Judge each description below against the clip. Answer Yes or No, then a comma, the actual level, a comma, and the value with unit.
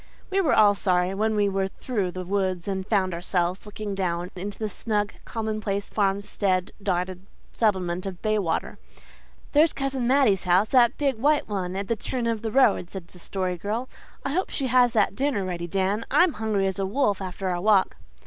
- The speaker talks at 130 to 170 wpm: No, average, 190 wpm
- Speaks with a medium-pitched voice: No, high, 200 Hz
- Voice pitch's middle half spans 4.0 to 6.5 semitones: No, average, 3.2 semitones